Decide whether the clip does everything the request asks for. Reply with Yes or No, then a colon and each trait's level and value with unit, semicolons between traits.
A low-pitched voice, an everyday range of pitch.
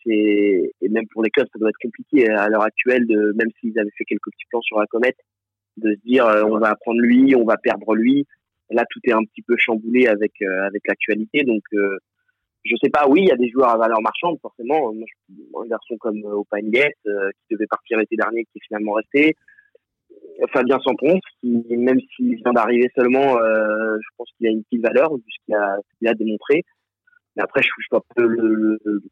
Yes: low, 115 Hz; average, 3.1 semitones